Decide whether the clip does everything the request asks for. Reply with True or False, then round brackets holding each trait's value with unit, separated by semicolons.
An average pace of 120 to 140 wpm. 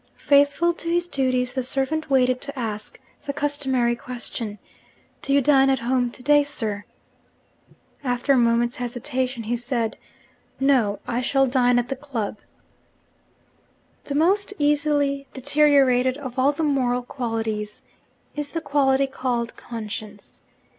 True (135 wpm)